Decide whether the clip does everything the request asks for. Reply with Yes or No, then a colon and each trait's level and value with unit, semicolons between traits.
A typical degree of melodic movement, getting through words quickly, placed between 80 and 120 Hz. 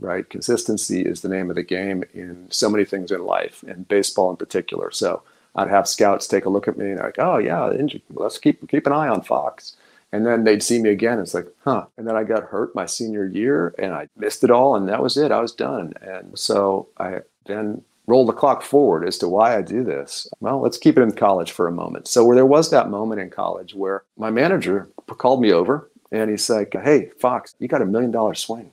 No: narrow, 2.3 semitones; fast, 240 wpm; low, 105 Hz